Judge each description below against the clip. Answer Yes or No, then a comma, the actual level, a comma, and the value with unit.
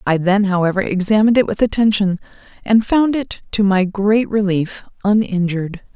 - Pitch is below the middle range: No, high, 200 Hz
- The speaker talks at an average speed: Yes, average, 150 wpm